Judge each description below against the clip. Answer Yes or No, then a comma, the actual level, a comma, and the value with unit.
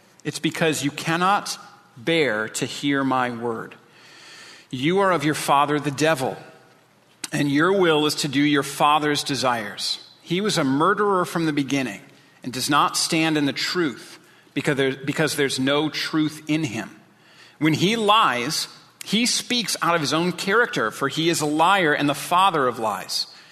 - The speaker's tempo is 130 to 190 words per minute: Yes, average, 170 wpm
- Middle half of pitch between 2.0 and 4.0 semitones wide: Yes, average, 3.3 semitones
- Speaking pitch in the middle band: Yes, medium, 150 Hz